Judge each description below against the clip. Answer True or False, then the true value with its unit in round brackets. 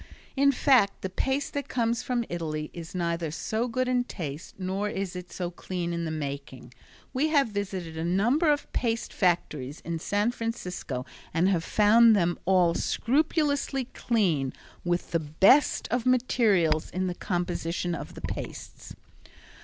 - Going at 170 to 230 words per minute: False (155 wpm)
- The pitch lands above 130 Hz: True (190 Hz)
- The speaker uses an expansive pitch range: True (6.0 semitones)